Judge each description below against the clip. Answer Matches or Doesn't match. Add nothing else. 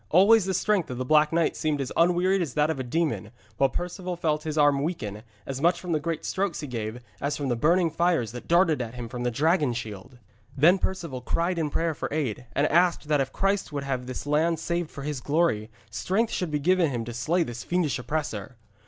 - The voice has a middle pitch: Matches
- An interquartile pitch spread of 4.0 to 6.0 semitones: Matches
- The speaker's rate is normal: Doesn't match